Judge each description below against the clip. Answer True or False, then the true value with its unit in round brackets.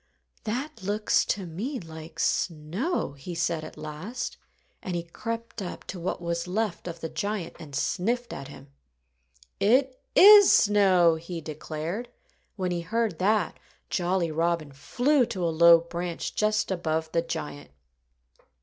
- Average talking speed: True (145 wpm)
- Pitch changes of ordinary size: True (4.7 semitones)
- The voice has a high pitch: False (175 Hz)